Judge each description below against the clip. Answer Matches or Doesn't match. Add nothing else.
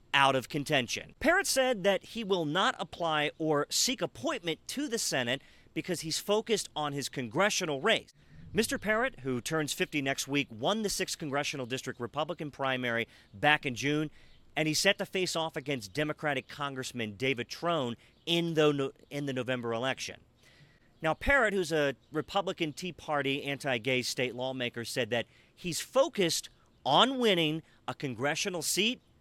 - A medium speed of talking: Matches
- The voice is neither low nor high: Matches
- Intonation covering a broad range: Matches